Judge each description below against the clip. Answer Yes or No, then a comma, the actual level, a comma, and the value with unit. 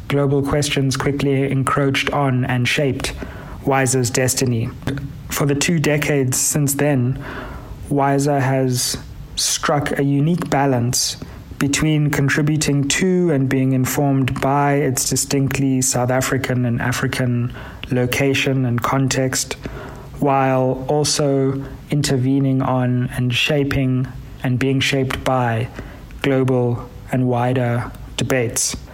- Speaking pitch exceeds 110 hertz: Yes, low, 135 Hz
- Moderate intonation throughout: No, narrow, 1.7 semitones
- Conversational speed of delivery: No, slow, 105 wpm